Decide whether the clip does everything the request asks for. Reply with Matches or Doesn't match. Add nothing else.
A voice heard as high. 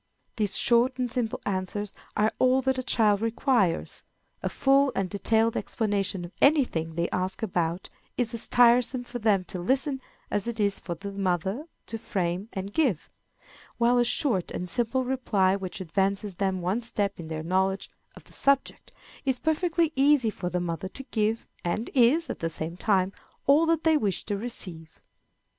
Matches